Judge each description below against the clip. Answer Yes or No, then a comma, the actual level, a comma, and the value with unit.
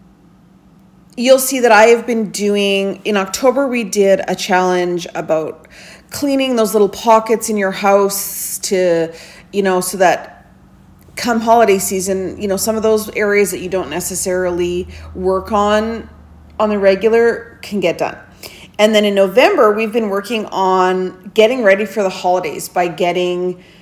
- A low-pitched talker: No, high, 195 Hz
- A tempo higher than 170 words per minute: No, average, 155 wpm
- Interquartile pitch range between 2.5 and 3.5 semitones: Yes, average, 3.0 semitones